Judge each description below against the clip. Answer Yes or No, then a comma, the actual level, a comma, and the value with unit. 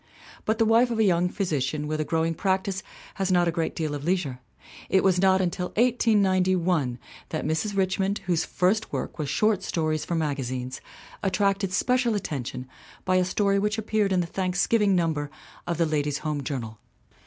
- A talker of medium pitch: Yes, medium, 180 Hz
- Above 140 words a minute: Yes, average, 175 wpm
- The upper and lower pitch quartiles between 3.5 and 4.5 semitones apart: Yes, average, 4.2 semitones